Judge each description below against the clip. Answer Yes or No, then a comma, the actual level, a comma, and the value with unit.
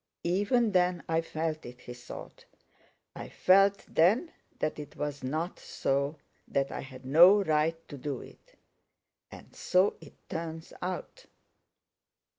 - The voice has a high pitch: No, medium, 160 Hz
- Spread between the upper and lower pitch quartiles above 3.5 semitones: Yes, average, 4.2 semitones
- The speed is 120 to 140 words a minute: Yes, slow, 135 wpm